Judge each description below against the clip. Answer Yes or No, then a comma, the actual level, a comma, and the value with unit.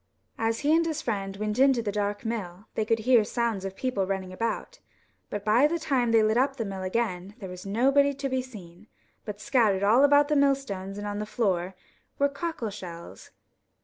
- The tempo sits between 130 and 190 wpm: No, fast, 205 wpm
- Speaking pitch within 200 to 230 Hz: Yes, high, 220 Hz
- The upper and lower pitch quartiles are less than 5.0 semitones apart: No, average, 5.3 semitones